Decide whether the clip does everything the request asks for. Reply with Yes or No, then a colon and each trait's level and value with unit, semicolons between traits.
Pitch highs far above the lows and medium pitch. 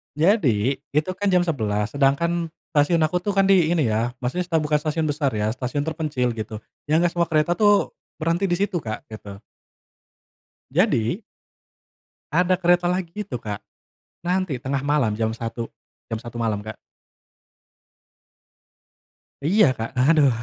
Yes: wide, 6.8 semitones; medium, 150 Hz